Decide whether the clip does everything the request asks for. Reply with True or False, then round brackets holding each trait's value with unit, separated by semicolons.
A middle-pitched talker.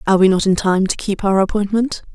False (200 Hz)